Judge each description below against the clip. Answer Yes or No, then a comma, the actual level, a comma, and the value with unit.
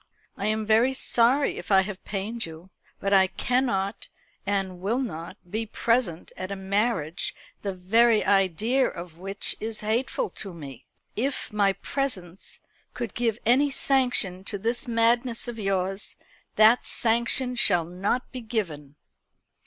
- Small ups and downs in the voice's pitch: No, average, 3.9 semitones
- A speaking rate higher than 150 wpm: No, average, 145 wpm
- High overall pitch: Yes, high, 210 Hz